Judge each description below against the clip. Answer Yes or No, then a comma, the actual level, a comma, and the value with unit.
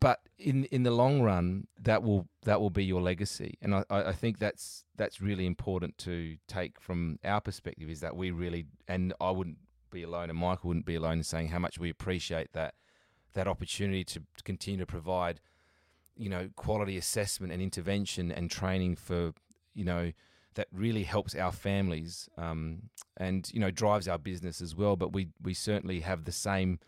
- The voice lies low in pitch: Yes, very low, 90 Hz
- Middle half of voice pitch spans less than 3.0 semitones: Yes, narrow, 2.6 semitones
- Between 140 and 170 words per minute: No, average, 190 wpm